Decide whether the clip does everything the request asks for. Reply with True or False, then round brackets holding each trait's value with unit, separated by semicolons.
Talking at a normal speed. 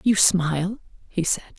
True (150 wpm)